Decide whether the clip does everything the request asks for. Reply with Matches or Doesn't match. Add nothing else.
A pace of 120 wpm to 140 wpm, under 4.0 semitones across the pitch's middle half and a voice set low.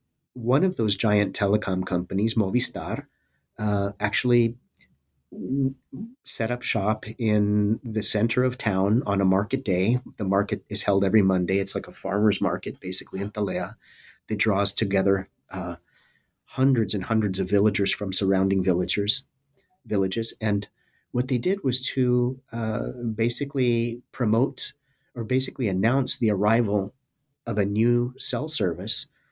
Matches